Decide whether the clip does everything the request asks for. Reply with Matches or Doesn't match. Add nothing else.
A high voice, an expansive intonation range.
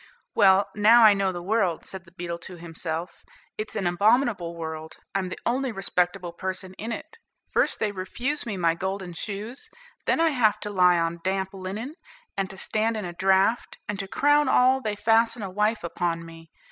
Doesn't match